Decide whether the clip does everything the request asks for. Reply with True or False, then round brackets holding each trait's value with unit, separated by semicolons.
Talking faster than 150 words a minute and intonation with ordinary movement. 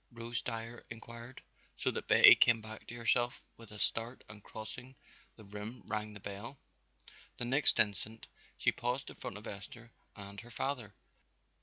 False (165 wpm; 2.2 semitones)